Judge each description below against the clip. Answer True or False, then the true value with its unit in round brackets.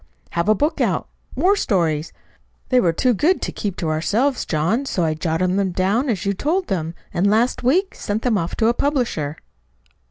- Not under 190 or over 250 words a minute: True (200 wpm)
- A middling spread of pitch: False (6.9 semitones)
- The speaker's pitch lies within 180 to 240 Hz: True (200 Hz)